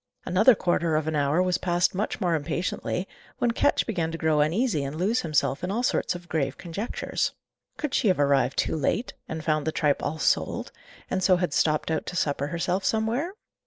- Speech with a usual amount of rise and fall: Yes, average, 3.7 semitones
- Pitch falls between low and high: Yes, medium, 170 Hz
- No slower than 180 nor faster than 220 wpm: Yes, average, 200 wpm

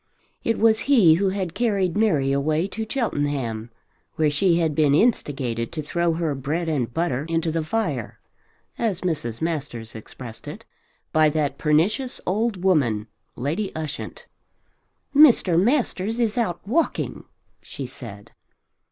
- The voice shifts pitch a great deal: Yes, wide, 6.2 semitones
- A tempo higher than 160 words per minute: No, slow, 135 wpm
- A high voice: No, medium, 165 Hz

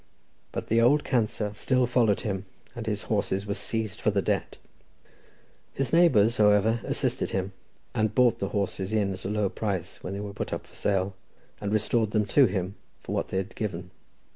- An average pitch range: No, narrow, 2.3 semitones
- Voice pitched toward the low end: Yes, low, 105 Hz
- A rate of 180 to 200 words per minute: Yes, average, 190 wpm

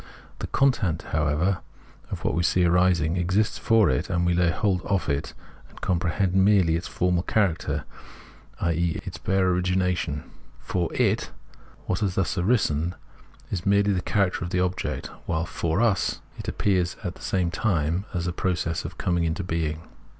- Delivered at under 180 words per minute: Yes, average, 165 wpm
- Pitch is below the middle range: Yes, very low, 90 Hz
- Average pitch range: No, narrow, 2.2 semitones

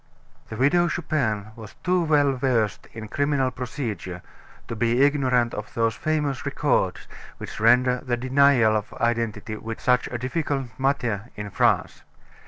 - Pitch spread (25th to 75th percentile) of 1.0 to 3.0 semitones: No, average, 4.1 semitones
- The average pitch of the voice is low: Yes, low, 125 Hz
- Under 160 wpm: Yes, average, 140 wpm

